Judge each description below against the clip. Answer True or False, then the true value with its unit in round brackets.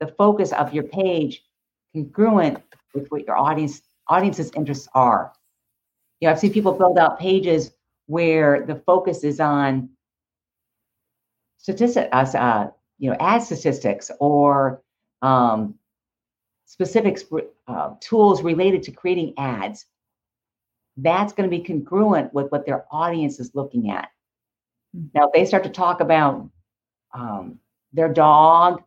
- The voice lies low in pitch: False (150 Hz)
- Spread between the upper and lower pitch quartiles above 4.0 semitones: True (5.5 semitones)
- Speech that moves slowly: True (130 wpm)